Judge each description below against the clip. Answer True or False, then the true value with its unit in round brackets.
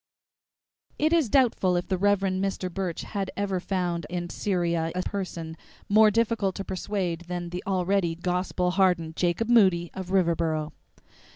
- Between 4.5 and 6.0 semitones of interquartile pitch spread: False (2.4 semitones)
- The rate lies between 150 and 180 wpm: True (155 wpm)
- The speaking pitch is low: False (185 Hz)